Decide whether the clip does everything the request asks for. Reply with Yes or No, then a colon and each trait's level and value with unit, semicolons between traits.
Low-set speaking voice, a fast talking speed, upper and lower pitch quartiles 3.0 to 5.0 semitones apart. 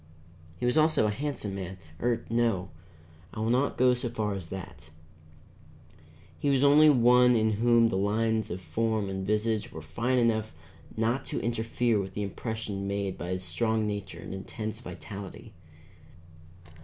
No: low, 110 Hz; average, 160 wpm; average, 3.4 semitones